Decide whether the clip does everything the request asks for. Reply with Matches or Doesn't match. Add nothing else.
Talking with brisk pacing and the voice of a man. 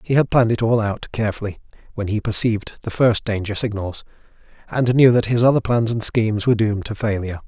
Matches